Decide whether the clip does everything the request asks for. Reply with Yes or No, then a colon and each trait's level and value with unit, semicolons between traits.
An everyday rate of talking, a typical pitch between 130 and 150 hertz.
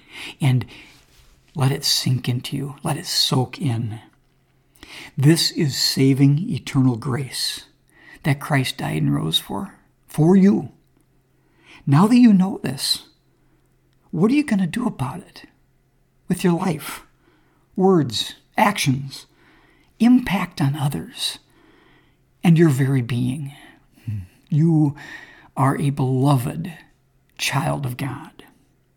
No: slow, 115 wpm; medium, 140 Hz